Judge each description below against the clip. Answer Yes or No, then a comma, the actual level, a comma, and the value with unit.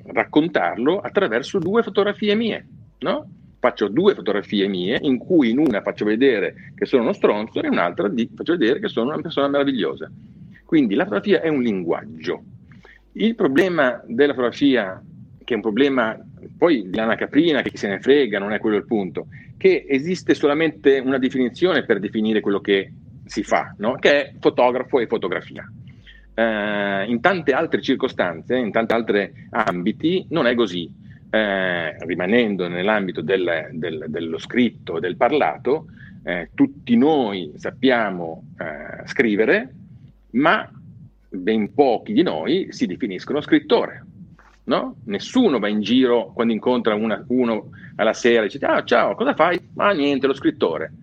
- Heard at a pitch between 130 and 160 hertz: Yes, low, 135 Hz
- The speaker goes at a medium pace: Yes, average, 160 wpm